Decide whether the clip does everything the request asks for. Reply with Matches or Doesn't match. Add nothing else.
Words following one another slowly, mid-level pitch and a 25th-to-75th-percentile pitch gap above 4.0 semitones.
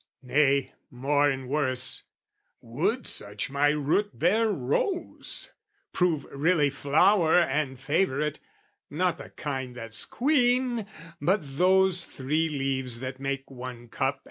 Matches